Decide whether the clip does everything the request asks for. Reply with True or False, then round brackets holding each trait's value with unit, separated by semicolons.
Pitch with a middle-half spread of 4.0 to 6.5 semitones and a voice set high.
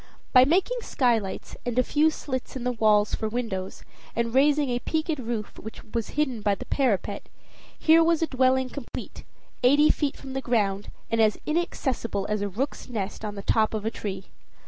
True (4.7 semitones; 245 Hz)